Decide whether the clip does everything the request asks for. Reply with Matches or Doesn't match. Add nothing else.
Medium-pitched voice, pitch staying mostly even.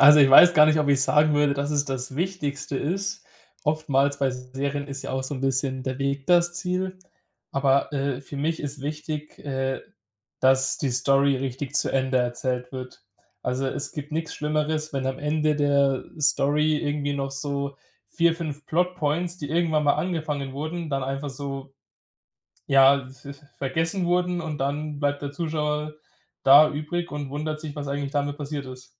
Matches